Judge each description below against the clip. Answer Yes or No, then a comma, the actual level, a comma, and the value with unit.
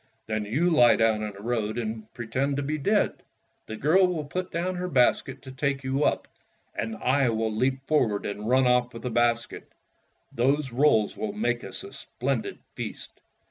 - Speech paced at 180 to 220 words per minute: Yes, average, 185 wpm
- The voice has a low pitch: Yes, low, 130 Hz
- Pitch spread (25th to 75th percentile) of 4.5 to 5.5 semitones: Yes, average, 4.9 semitones